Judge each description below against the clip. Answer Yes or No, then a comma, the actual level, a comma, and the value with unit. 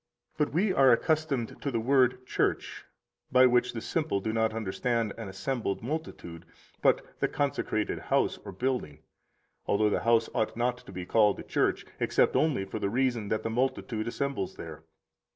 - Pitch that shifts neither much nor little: Yes, average, 4.0 semitones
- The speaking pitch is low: Yes, low, 115 Hz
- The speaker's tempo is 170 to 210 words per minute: Yes, average, 175 wpm